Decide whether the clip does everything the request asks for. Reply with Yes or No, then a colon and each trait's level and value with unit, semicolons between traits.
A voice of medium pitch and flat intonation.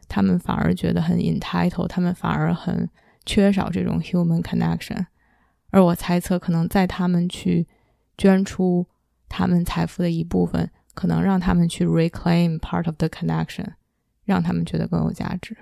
Yes: medium, 175 Hz; narrow, 2.1 semitones